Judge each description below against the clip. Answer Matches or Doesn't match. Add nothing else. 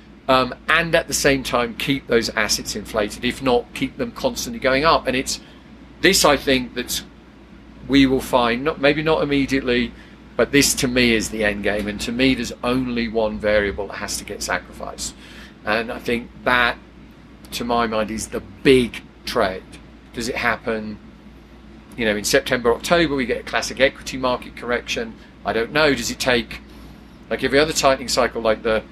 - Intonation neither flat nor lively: Matches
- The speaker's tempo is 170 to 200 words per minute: Matches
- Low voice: Matches